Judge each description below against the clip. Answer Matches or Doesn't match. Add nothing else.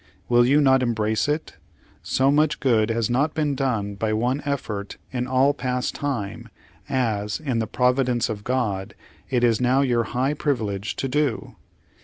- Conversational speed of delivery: Matches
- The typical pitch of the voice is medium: Doesn't match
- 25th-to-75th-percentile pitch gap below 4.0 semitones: Matches